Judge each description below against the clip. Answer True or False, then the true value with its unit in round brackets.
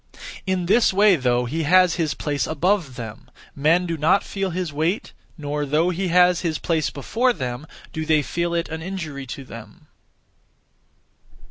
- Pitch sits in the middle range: True (160 Hz)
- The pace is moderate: True (165 wpm)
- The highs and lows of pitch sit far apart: False (3.9 semitones)